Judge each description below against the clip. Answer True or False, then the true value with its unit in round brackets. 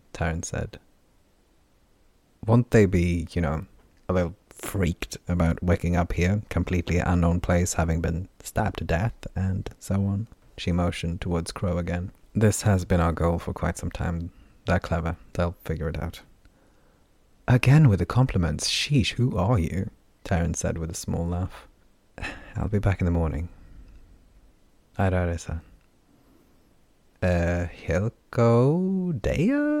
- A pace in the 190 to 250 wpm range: False (145 wpm)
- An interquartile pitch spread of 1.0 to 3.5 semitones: True (3.1 semitones)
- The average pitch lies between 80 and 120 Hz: True (90 Hz)